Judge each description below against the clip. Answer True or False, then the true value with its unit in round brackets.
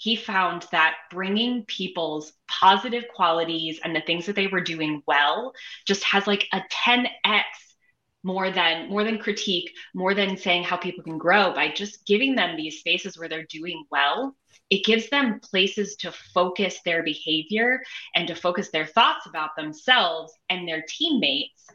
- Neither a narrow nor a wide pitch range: True (4.3 semitones)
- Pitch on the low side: False (185 Hz)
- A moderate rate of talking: True (165 wpm)